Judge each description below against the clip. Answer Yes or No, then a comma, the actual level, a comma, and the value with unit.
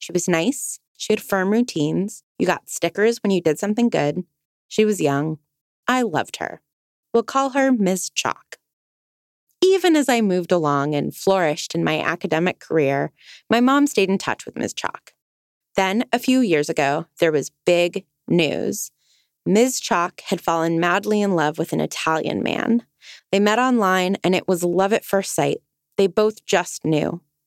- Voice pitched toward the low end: No, high, 190 Hz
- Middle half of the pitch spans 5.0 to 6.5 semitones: Yes, wide, 5.6 semitones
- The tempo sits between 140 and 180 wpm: Yes, average, 175 wpm